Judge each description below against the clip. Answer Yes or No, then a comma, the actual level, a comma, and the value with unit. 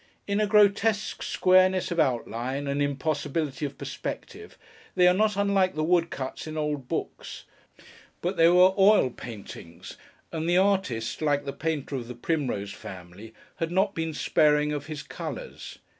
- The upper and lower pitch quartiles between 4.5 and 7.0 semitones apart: Yes, average, 5.3 semitones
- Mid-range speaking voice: Yes, medium, 155 Hz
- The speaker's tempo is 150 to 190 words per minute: Yes, average, 155 wpm